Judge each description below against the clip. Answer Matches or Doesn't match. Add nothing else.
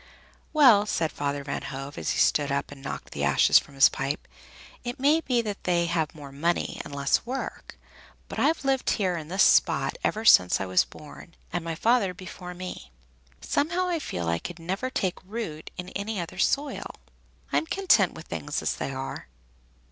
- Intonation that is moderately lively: Doesn't match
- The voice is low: Doesn't match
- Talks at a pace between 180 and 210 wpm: Matches